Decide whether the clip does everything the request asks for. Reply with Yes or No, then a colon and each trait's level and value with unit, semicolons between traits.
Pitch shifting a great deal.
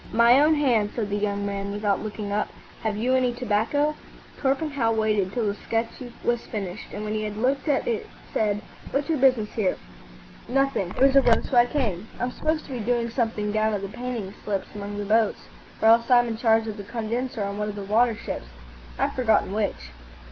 No: average, 3.2 semitones